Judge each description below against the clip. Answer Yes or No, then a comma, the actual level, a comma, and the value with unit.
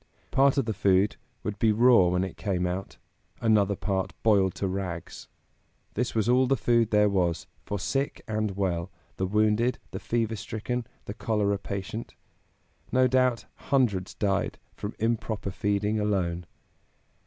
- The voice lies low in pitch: Yes, low, 105 Hz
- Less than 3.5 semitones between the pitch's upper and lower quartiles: Yes, average, 3.1 semitones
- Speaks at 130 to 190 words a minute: Yes, average, 150 wpm